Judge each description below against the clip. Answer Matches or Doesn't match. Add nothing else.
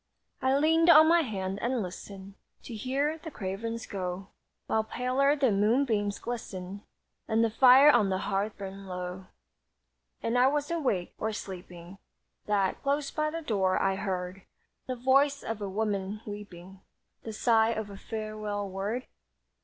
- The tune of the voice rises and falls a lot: Doesn't match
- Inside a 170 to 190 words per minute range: Doesn't match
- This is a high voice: Matches